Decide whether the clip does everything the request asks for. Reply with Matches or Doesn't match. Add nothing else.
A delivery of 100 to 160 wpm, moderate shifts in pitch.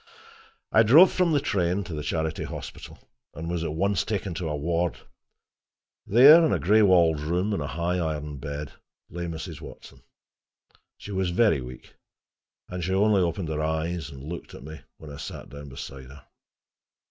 Doesn't match